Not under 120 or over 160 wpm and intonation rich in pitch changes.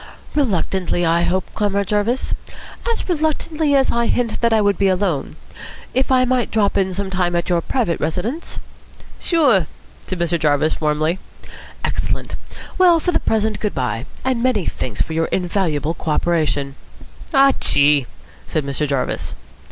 Yes: average, 155 wpm; wide, 7.2 semitones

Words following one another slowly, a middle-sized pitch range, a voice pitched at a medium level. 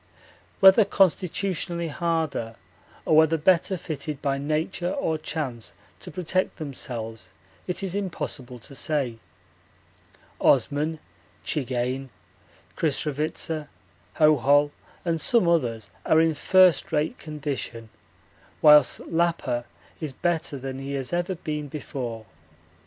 Yes: slow, 110 wpm; average, 3.9 semitones; medium, 150 Hz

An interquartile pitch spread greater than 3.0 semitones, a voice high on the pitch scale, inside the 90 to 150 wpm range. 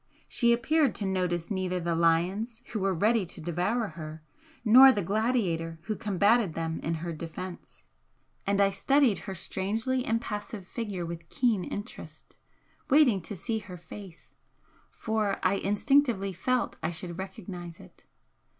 Yes: average, 4.6 semitones; high, 195 Hz; average, 145 wpm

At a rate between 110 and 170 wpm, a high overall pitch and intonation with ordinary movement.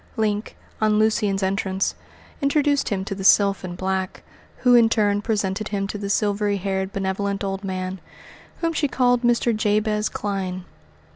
No: average, 160 wpm; high, 205 Hz; narrow, 2.0 semitones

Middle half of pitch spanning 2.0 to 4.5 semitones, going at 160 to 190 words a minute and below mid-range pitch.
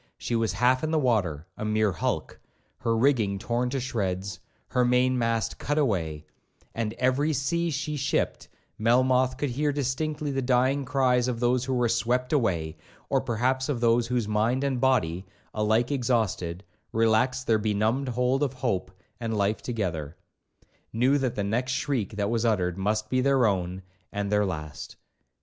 Yes: average, 3.7 semitones; average, 165 wpm; low, 120 Hz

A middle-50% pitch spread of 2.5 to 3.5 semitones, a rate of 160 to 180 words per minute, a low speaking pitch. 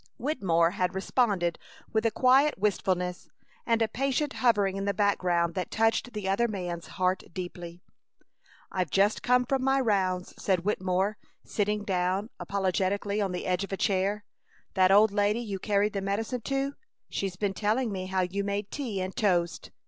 No: average, 3.0 semitones; average, 170 wpm; high, 200 Hz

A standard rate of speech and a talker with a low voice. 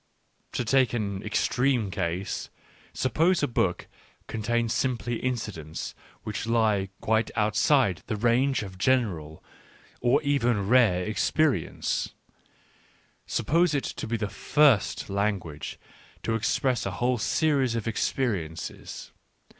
No: slow, 120 wpm; low, 115 Hz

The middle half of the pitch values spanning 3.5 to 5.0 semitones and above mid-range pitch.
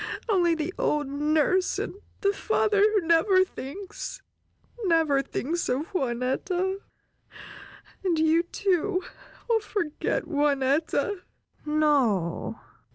Yes: average, 4.7 semitones; very high, 330 Hz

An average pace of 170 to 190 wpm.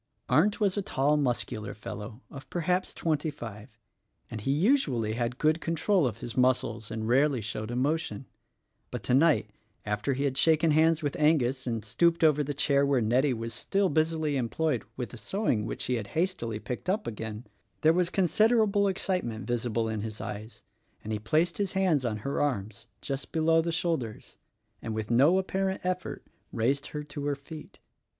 Yes: average, 185 wpm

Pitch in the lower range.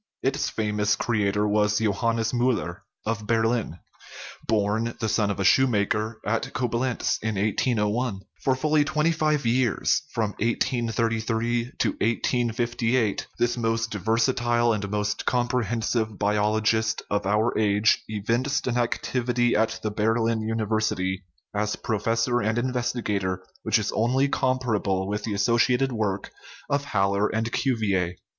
Yes: low, 115 Hz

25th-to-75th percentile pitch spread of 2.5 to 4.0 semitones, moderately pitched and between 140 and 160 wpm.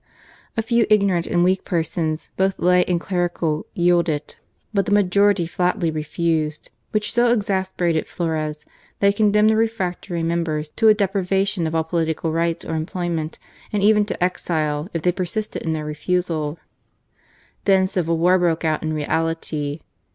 Yes: average, 3.4 semitones; medium, 175 Hz; average, 155 wpm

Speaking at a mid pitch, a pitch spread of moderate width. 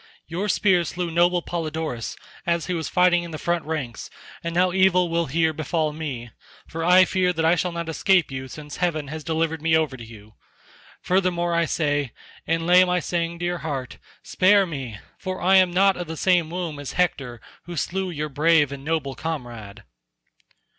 Yes: medium, 165 Hz; average, 3.1 semitones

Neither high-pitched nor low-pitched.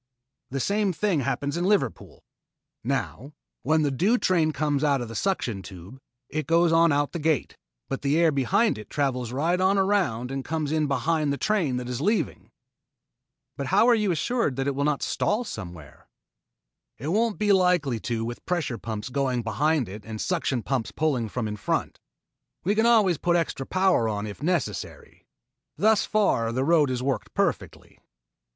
Yes: medium, 145 Hz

